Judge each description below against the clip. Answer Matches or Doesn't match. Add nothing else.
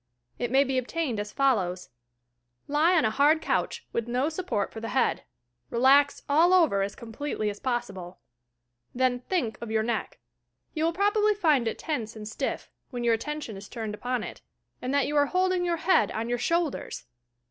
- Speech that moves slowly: Doesn't match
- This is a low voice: Doesn't match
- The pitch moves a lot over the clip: Matches